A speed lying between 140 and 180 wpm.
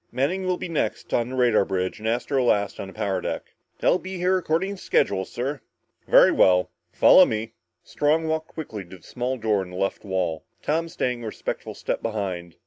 No: fast, 205 wpm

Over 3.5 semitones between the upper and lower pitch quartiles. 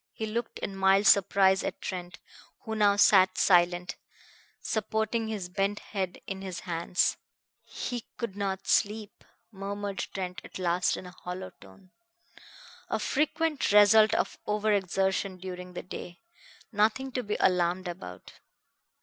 No: average, 2.7 semitones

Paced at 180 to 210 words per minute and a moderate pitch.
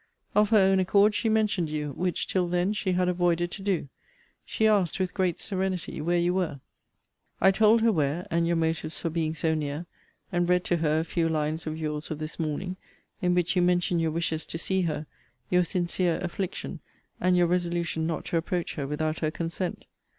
Yes: average, 200 wpm; medium, 175 Hz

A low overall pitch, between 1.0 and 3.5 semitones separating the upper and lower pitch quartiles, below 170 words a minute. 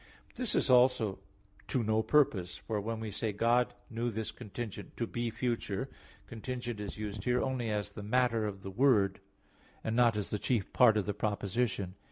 No: low, 110 Hz; average, 2.9 semitones; average, 190 wpm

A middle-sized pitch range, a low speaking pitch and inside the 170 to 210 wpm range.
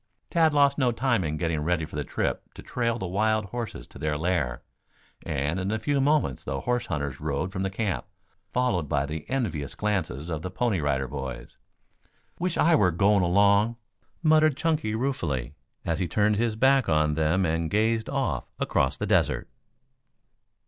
No: wide, 7.6 semitones; very low, 95 Hz; average, 175 wpm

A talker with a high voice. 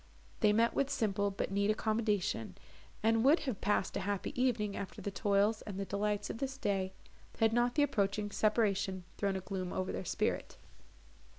Yes: high, 205 Hz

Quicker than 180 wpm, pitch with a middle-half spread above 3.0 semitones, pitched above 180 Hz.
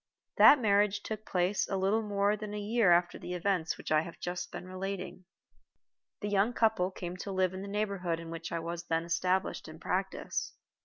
No: fast, 205 wpm; average, 2.7 semitones; high, 190 Hz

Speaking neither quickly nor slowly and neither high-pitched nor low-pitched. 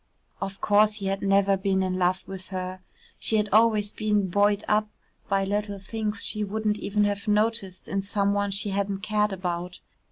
No: average, 185 wpm; high, 200 Hz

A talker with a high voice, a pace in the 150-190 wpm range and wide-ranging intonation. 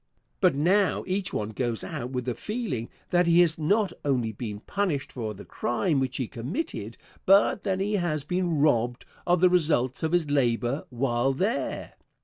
No: medium, 145 Hz; average, 175 wpm; wide, 6.9 semitones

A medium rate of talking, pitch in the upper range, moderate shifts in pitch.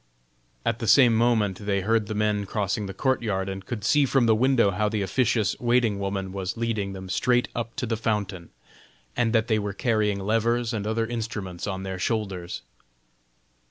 No: average, 185 wpm; low, 105 Hz; average, 3.0 semitones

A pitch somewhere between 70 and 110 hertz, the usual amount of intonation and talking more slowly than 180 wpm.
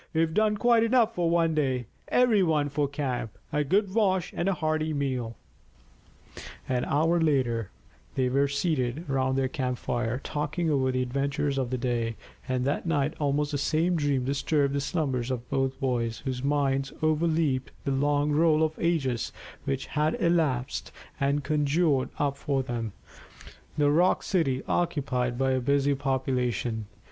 No: medium, 140 Hz; average, 3.3 semitones; average, 160 wpm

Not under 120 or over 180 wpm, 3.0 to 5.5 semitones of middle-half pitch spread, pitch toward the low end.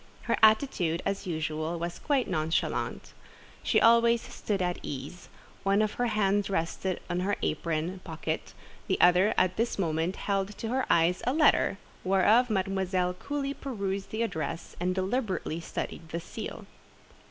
No: average, 150 wpm; average, 4.1 semitones; high, 190 Hz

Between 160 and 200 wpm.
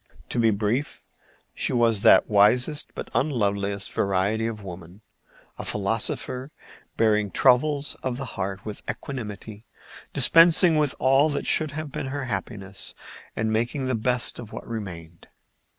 No: average, 140 wpm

